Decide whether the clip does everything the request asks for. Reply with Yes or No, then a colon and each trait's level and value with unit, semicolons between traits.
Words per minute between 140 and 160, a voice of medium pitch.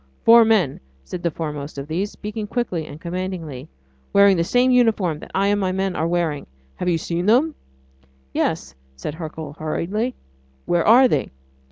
No: average, 170 wpm; medium, 180 Hz